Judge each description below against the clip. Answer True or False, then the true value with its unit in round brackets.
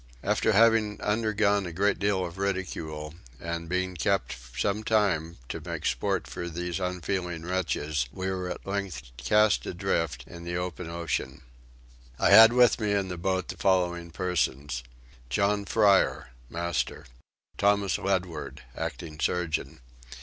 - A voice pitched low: True (90 Hz)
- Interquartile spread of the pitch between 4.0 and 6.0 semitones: False (3.2 semitones)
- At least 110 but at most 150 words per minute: True (140 wpm)